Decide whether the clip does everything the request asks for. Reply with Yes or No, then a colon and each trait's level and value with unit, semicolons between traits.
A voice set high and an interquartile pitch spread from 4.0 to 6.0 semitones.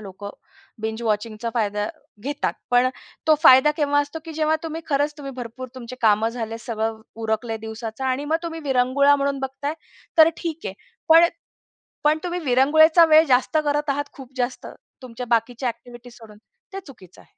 Yes: very high, 255 Hz; average, 4.5 semitones